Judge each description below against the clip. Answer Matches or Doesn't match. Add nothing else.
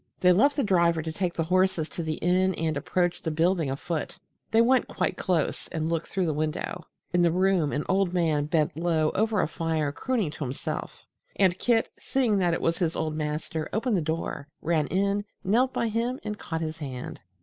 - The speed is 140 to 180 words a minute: Doesn't match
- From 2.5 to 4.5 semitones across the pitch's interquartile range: Matches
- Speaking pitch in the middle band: Matches